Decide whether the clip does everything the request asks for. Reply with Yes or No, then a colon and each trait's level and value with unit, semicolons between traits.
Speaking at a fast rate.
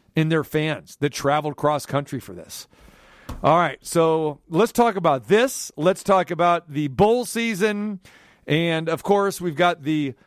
No: average, 165 wpm